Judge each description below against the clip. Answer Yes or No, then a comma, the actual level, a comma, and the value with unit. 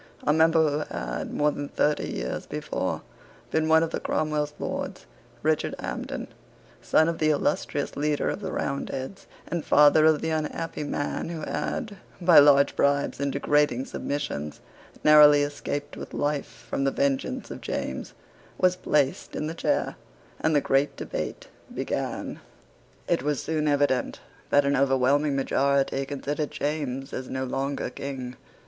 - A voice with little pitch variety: Yes, narrow, 1.8 semitones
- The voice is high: No, medium, 145 Hz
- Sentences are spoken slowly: No, average, 150 wpm